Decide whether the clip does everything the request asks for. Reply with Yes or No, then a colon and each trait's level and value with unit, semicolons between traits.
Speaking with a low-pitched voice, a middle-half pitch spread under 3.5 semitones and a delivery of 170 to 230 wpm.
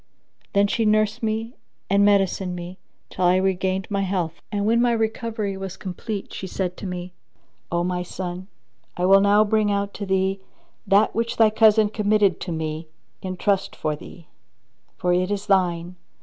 No: high, 195 Hz; average, 2.7 semitones; average, 175 wpm